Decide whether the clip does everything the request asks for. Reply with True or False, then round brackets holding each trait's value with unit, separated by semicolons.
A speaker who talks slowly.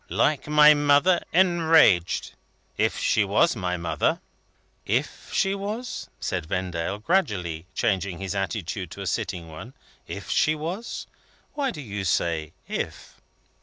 True (130 wpm)